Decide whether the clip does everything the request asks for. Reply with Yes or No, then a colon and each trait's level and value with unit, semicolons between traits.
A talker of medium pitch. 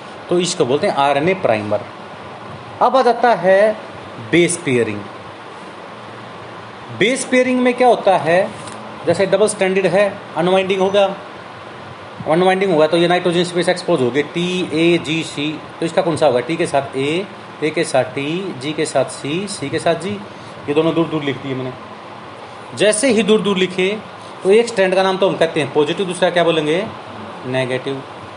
Yes: medium, 170 Hz